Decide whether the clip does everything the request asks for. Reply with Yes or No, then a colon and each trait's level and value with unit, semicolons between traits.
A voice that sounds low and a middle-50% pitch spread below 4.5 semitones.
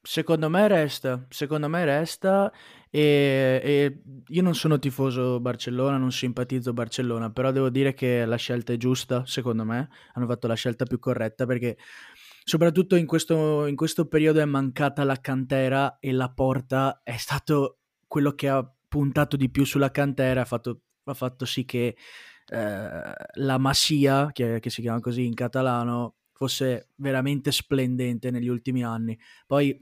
Yes: low, 130 Hz; narrow, 2.5 semitones